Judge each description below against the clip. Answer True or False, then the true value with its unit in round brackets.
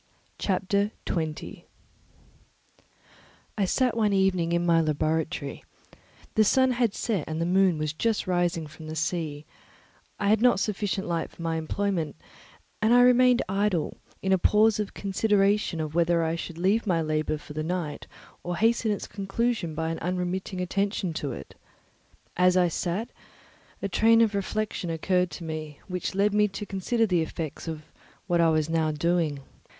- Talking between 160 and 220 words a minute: True (165 wpm)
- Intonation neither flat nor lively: True (4.1 semitones)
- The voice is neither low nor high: True (180 Hz)